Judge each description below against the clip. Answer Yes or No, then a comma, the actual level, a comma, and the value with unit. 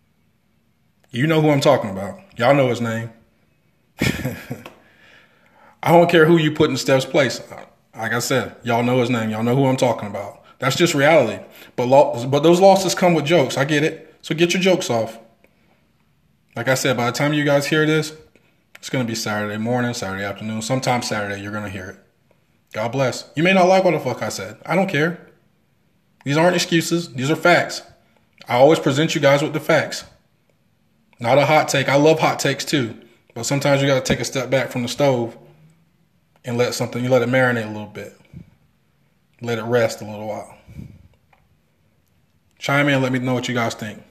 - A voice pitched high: No, low, 135 Hz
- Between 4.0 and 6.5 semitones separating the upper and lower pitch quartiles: Yes, average, 5.1 semitones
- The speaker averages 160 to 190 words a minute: No, fast, 205 wpm